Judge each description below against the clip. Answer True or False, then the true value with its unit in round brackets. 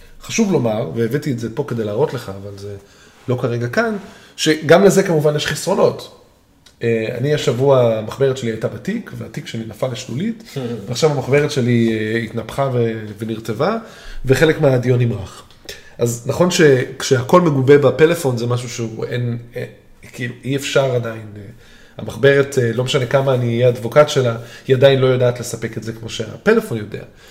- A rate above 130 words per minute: True (150 wpm)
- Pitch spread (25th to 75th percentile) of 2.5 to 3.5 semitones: False (4.1 semitones)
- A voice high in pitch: False (125 Hz)